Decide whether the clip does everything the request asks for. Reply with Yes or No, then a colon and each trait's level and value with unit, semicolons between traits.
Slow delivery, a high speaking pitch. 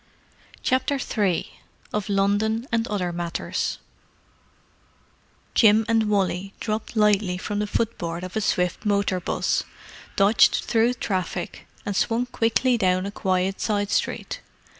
Yes: slow, 130 wpm; high, 205 Hz